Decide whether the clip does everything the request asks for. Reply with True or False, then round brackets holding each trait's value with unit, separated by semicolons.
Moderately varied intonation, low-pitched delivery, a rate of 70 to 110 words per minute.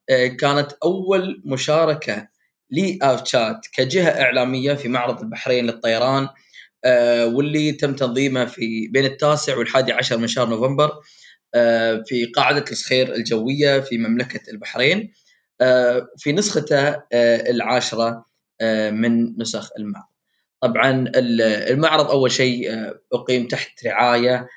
True (3.3 semitones; 125 Hz; 100 wpm)